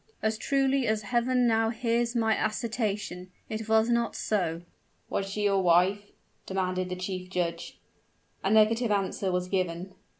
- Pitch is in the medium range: No, high, 210 Hz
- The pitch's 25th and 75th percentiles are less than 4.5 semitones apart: Yes, average, 3.7 semitones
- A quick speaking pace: No, average, 145 wpm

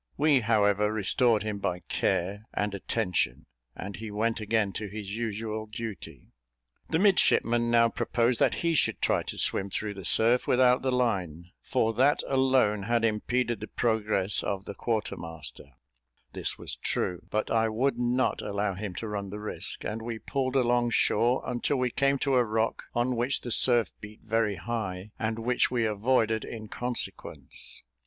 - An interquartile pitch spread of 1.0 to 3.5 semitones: Yes, average, 2.8 semitones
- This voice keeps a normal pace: Yes, average, 170 wpm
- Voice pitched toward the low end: Yes, low, 110 Hz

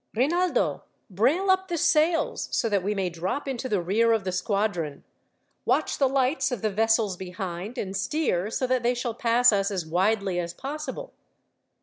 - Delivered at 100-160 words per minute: No, average, 180 wpm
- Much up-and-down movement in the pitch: Yes, wide, 5.8 semitones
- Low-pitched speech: No, high, 225 Hz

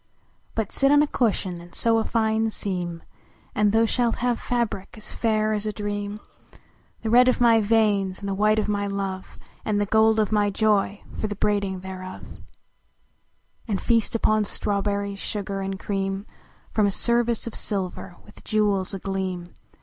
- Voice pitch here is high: Yes, high, 205 Hz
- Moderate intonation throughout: No, narrow, 2.1 semitones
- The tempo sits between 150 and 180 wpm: Yes, average, 170 wpm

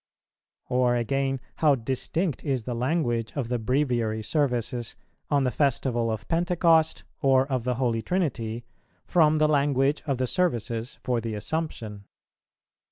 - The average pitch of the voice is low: Yes, low, 130 Hz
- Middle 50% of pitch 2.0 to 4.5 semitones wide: Yes, average, 4.1 semitones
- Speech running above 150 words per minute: No, average, 140 wpm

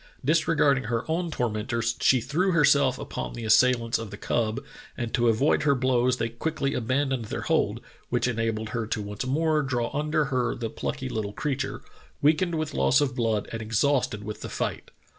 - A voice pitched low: Yes, low, 125 Hz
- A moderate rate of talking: Yes, average, 180 wpm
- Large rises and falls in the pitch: No, average, 4.1 semitones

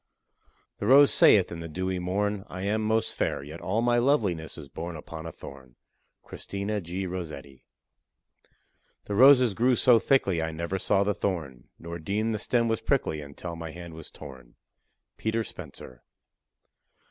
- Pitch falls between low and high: No, very low, 95 Hz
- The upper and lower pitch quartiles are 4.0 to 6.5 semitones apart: Yes, average, 5.2 semitones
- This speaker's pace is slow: No, average, 160 wpm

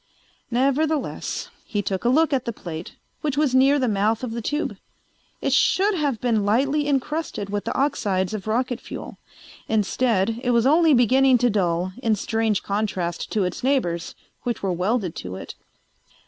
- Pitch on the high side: Yes, high, 235 Hz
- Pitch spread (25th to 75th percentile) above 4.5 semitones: Yes, average, 5.1 semitones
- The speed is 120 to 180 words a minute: Yes, average, 170 wpm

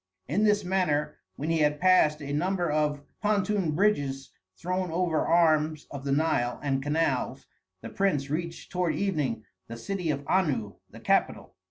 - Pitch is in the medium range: Yes, medium, 155 Hz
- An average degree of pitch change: Yes, average, 4.2 semitones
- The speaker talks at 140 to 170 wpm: Yes, average, 160 wpm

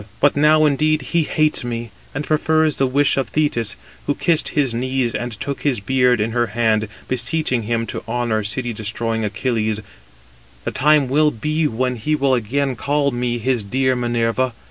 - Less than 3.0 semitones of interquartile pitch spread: No, average, 3.9 semitones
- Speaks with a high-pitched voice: No, low, 125 Hz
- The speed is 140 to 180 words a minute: Yes, average, 175 wpm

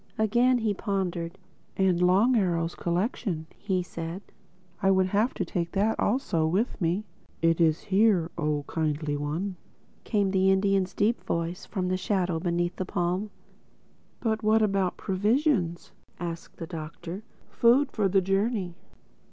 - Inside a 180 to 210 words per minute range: No, average, 140 wpm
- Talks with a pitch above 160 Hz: Yes, medium, 185 Hz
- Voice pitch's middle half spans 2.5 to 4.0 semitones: Yes, average, 3.4 semitones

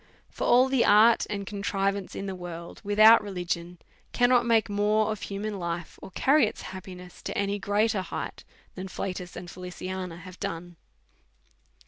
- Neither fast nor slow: Yes, average, 155 wpm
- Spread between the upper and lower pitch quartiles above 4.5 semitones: No, average, 2.9 semitones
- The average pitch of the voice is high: Yes, high, 195 Hz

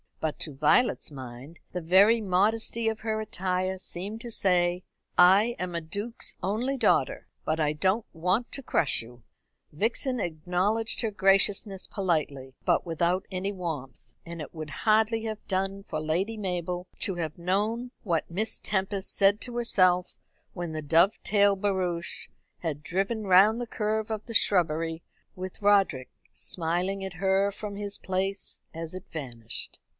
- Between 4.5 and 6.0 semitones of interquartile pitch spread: No, average, 3.9 semitones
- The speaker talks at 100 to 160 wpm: Yes, average, 150 wpm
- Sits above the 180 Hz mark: Yes, high, 190 Hz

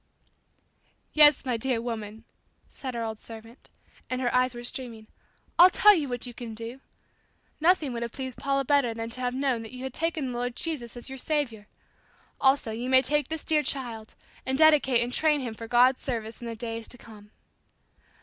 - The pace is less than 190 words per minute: No, average, 200 wpm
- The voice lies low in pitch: No, very high, 250 Hz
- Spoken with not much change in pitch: No, average, 3.1 semitones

